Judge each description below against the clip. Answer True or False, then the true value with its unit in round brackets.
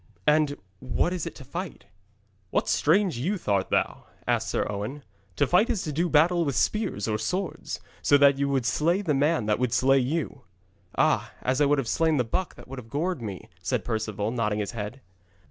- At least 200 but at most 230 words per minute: True (205 wpm)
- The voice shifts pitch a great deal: True (6.2 semitones)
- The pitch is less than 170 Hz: True (140 Hz)